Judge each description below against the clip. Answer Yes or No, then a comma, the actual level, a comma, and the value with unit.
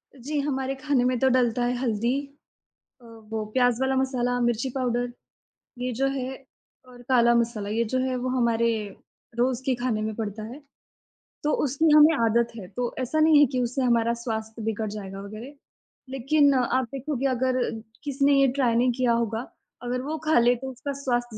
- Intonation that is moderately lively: No, narrow, 2.3 semitones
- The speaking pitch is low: No, high, 245 Hz